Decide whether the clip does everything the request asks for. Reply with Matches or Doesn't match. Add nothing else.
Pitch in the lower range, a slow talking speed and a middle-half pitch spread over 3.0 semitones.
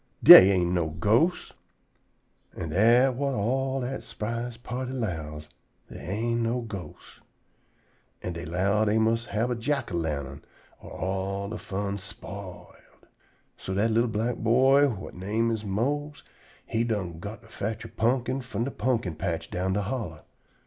Doesn't match